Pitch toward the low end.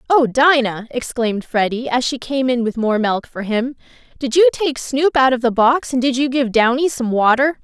No: very high, 255 Hz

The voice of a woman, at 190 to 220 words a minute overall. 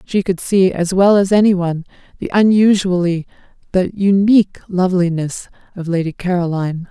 No: female; average, 140 wpm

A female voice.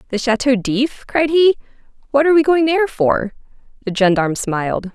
Yes: female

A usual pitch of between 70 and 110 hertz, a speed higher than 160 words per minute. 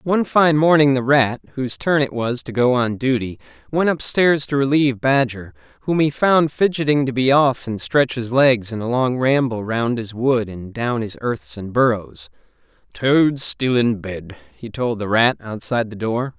No: low, 125 Hz; average, 195 wpm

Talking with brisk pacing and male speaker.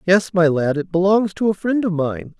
Yes: fast, 250 wpm; male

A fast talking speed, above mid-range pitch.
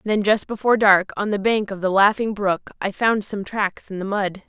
Yes: fast, 240 wpm; high, 205 Hz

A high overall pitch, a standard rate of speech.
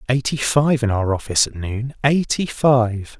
No: low, 125 Hz; average, 150 wpm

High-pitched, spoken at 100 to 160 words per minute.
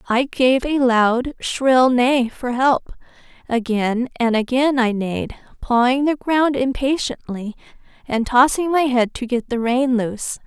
Yes: very high, 250 Hz; average, 150 wpm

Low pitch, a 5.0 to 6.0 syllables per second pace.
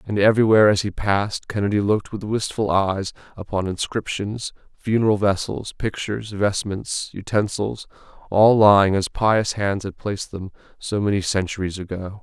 Yes: low, 100 Hz; 5.1 syllables/s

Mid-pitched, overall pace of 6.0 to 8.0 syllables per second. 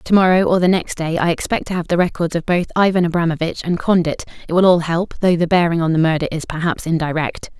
Yes: medium, 170 Hz; 6.3 syllables/s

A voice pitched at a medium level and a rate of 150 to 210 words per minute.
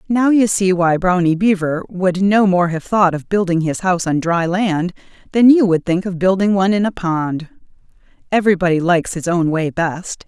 Yes: medium, 180 Hz; average, 200 wpm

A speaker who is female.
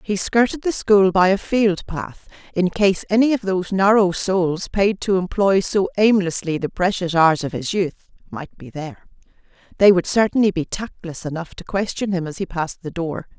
Yes: female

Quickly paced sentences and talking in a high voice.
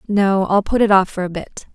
Yes: fast, 275 wpm; high, 195 Hz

